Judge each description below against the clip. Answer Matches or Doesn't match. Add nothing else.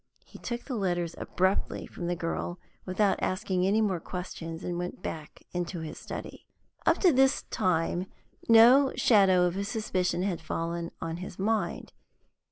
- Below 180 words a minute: Matches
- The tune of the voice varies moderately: Matches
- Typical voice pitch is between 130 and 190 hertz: Matches